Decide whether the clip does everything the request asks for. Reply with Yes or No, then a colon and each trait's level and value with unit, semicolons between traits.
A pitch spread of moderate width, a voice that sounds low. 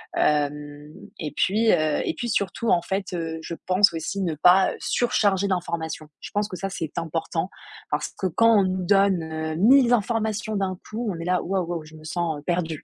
No: average, 3.7 semitones; medium, 180 Hz